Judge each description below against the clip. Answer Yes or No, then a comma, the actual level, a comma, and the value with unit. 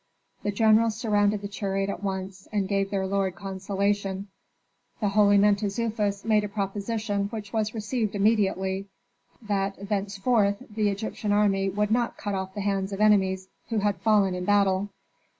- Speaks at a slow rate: No, average, 155 wpm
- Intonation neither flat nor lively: No, narrow, 1.3 semitones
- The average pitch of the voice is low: No, high, 200 Hz